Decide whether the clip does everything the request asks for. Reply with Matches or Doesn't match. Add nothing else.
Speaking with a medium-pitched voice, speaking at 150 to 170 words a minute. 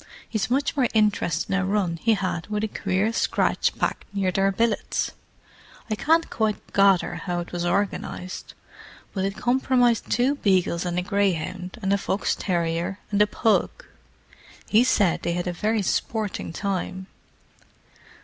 Doesn't match